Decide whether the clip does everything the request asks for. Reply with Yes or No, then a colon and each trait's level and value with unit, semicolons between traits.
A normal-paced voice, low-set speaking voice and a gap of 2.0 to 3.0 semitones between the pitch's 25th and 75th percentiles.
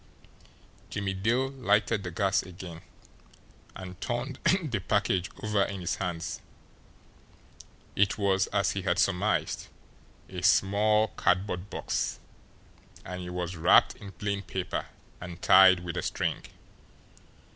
No: slow, 125 wpm; very low, 95 Hz; narrow, 2.6 semitones